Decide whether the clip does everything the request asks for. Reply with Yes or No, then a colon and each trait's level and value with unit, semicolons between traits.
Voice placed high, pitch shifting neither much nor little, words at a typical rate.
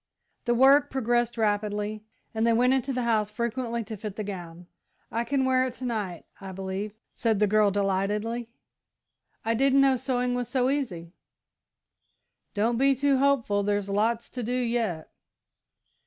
Yes: high, 230 Hz; average, 3.4 semitones; average, 160 wpm